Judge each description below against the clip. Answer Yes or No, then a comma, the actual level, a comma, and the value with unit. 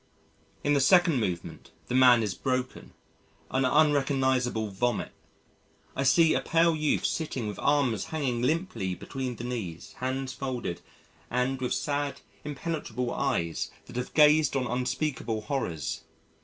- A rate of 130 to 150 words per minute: Yes, slow, 135 wpm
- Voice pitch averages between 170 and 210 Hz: No, low, 130 Hz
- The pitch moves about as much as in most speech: Yes, average, 3.3 semitones